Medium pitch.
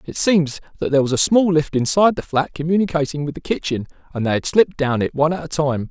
Yes: medium, 155 Hz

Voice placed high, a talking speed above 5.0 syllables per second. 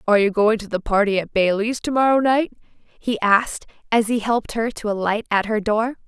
Yes: high, 220 Hz; 5.4 syllables/s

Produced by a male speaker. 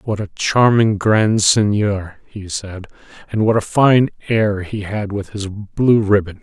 Yes: male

